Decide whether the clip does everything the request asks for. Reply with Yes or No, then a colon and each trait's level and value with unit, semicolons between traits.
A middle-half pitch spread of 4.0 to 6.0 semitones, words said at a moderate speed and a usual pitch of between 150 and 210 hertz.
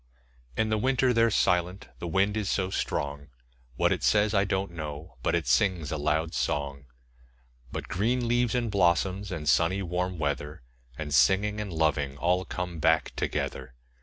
No: average, 5.1 semitones; average, 170 wpm; very low, 90 Hz